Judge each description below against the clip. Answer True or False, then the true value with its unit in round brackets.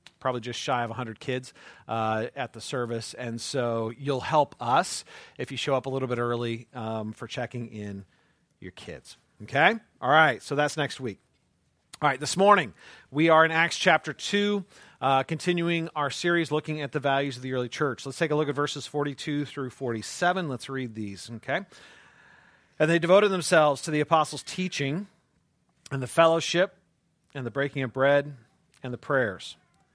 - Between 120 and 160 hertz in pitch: True (140 Hz)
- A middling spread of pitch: True (4.5 semitones)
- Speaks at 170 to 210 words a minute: True (180 wpm)